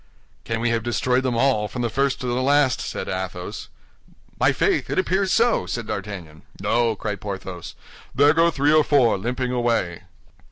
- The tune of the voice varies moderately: Yes, average, 4.8 semitones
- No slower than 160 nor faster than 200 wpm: Yes, average, 175 wpm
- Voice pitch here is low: Yes, low, 120 Hz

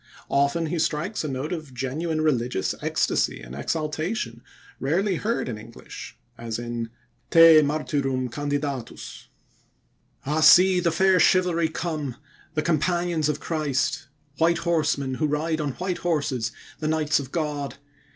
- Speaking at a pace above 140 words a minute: No, slow, 135 wpm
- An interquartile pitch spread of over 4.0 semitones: No, average, 3.6 semitones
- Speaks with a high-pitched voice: No, medium, 155 Hz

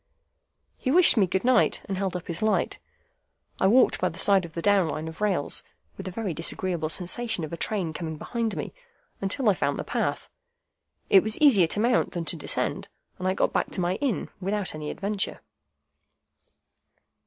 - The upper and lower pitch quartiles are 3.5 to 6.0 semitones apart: Yes, average, 4.1 semitones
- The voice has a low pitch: No, high, 190 Hz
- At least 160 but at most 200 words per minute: Yes, average, 190 wpm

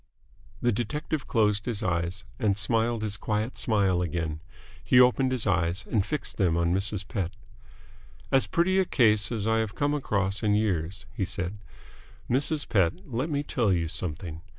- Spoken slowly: No, average, 170 wpm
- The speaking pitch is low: Yes, low, 105 Hz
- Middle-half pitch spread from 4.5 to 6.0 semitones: Yes, average, 4.8 semitones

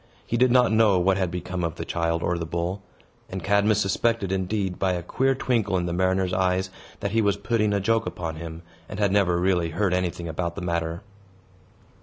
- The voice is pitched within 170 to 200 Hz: No, very low, 95 Hz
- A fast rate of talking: Yes, fast, 210 wpm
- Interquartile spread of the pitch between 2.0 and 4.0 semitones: Yes, average, 2.8 semitones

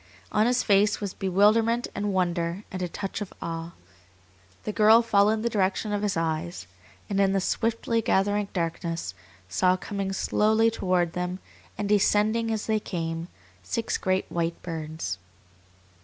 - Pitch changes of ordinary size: Yes, average, 3.5 semitones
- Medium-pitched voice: No, high, 195 Hz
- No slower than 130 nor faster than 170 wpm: Yes, average, 150 wpm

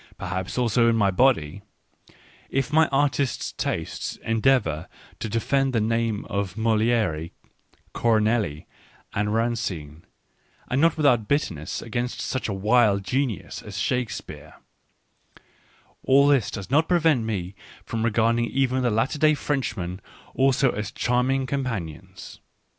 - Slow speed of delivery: Yes, slow, 130 wpm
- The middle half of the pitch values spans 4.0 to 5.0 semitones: Yes, average, 4.6 semitones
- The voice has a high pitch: No, low, 115 Hz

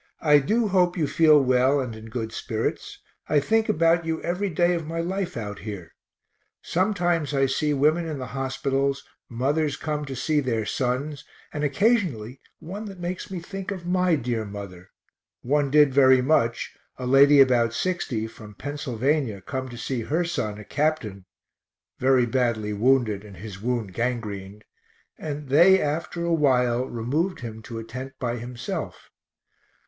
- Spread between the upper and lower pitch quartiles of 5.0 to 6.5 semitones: Yes, wide, 5.4 semitones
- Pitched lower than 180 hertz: Yes, low, 135 Hz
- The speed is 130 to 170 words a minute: Yes, average, 165 wpm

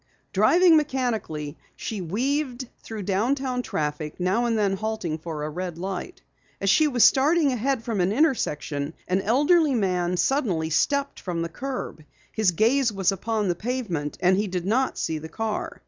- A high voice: Yes, high, 210 Hz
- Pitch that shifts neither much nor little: No, wide, 6.6 semitones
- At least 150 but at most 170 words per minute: Yes, average, 165 wpm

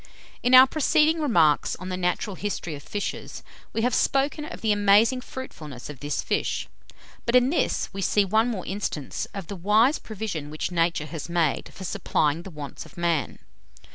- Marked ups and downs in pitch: Yes, wide, 6.1 semitones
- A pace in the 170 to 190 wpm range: Yes, average, 180 wpm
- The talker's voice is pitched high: Yes, high, 195 Hz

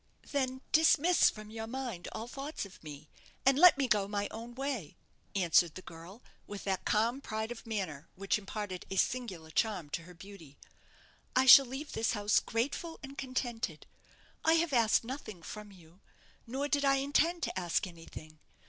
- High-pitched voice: Yes, high, 220 Hz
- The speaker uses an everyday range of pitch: No, wide, 6.2 semitones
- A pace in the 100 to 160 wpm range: No, average, 175 wpm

